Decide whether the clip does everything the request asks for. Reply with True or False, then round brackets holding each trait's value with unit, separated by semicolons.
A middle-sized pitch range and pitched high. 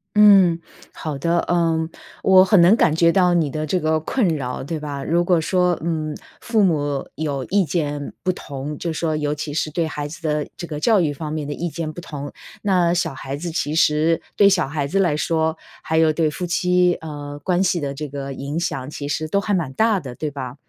False (3.2 semitones; 160 Hz)